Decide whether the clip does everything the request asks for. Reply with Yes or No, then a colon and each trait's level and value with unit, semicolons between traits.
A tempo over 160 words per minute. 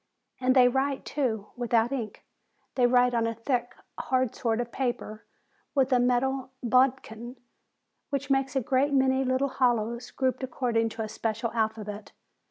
No: average, 155 wpm